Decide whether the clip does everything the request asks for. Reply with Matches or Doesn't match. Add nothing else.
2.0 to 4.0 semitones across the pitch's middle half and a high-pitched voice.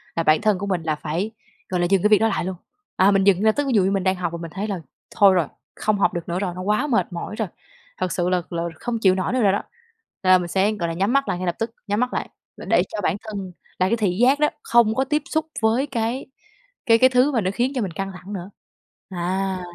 Matches